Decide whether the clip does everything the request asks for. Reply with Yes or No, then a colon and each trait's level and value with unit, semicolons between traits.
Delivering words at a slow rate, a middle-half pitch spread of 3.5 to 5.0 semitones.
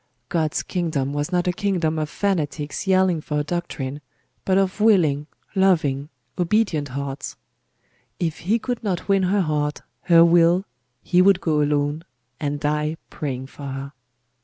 No: average, 150 wpm; average, 4.2 semitones